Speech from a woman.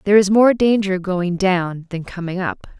Yes: female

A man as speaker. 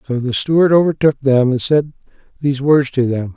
Yes: male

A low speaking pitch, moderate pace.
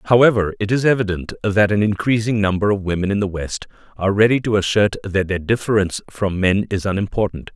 Yes: low, 100 Hz; average, 190 wpm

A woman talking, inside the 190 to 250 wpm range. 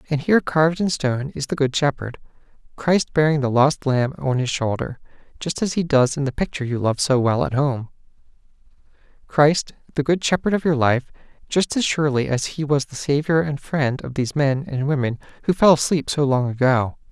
No: male; fast, 205 wpm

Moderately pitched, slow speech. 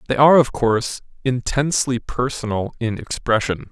No: low, 125 Hz; slow, 130 wpm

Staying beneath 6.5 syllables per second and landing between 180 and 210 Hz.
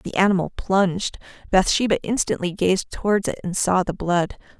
Yes: 5.1 syllables/s; high, 190 Hz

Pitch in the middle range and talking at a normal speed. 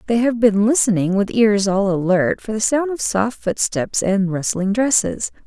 No: high, 205 Hz; average, 185 wpm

